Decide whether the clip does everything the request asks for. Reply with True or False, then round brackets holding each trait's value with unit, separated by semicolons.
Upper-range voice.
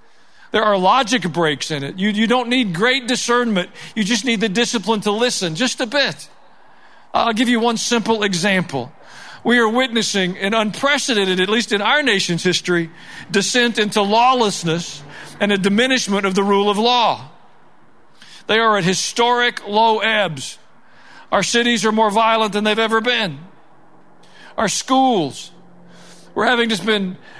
True (220 Hz)